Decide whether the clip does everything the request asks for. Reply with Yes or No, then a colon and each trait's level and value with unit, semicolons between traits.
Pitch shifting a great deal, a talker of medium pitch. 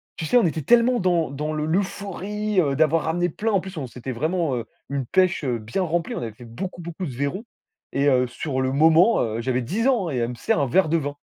Yes: wide, 6.0 semitones; medium, 160 Hz